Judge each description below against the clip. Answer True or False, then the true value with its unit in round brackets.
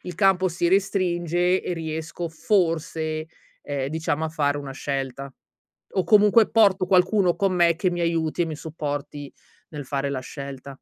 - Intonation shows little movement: False (3.9 semitones)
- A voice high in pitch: False (165 Hz)